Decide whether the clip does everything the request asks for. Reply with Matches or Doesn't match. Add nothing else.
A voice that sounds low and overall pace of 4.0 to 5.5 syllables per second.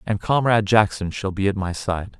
Matches